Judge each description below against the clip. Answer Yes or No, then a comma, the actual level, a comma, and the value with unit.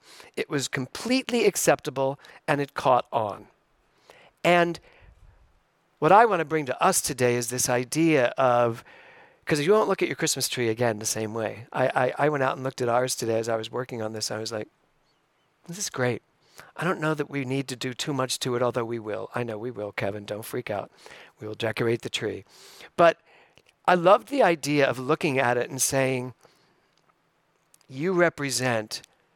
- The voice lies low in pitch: Yes, low, 130 Hz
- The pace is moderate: Yes, average, 195 wpm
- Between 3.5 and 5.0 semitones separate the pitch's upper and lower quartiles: No, wide, 5.5 semitones